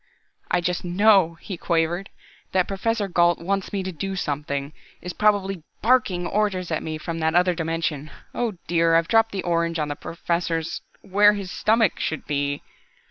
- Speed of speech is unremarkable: Yes, average, 170 wpm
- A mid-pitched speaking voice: Yes, medium, 175 Hz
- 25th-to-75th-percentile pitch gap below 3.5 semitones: Yes, average, 3.1 semitones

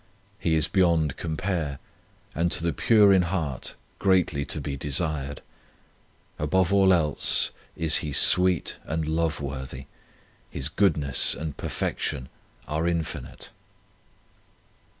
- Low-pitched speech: Yes, very low, 80 Hz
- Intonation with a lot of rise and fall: No, average, 3.4 semitones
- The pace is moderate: No, slow, 115 wpm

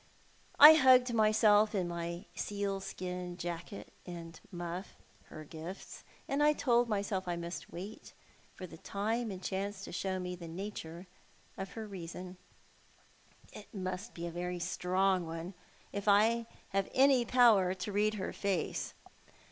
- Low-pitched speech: No, high, 190 Hz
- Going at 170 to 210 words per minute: No, average, 150 wpm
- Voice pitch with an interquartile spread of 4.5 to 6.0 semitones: No, average, 3.2 semitones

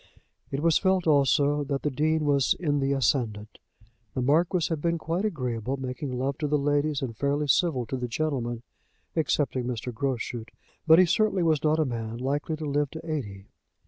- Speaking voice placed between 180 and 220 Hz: No, medium, 145 Hz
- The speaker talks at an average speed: Yes, average, 185 wpm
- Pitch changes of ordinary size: Yes, average, 3.6 semitones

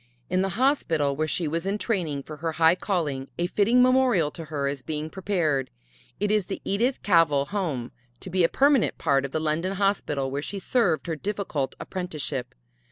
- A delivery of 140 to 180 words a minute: No, average, 190 wpm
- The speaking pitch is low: No, medium, 165 Hz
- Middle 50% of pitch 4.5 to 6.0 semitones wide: Yes, average, 5.2 semitones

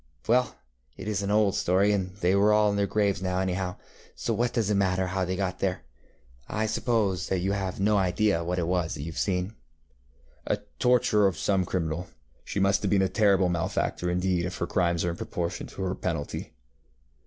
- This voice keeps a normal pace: No, fast, 210 wpm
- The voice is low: Yes, very low, 95 Hz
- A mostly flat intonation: Yes, narrow, 2.3 semitones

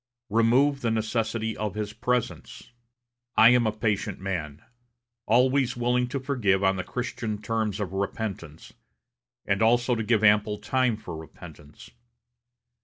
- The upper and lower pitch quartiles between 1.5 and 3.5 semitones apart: Yes, average, 3.1 semitones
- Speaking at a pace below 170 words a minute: Yes, slow, 135 wpm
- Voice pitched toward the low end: Yes, low, 110 Hz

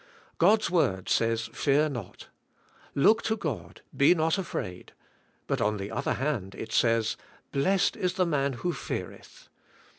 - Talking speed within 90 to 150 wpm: Yes, average, 145 wpm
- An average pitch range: No, wide, 7.7 semitones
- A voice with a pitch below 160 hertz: Yes, medium, 140 Hz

